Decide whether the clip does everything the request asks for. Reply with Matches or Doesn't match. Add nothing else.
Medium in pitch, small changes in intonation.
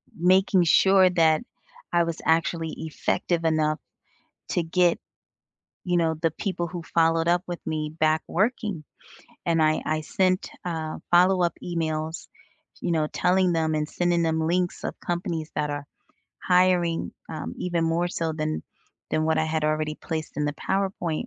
Matches